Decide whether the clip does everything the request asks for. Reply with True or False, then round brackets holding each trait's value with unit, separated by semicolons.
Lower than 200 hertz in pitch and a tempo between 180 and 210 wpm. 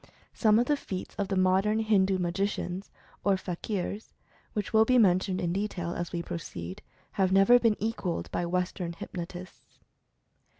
False (190 Hz; 160 wpm)